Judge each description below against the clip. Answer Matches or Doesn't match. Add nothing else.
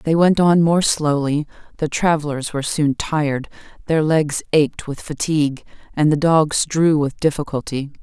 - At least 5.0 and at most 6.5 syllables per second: Doesn't match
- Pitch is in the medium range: Matches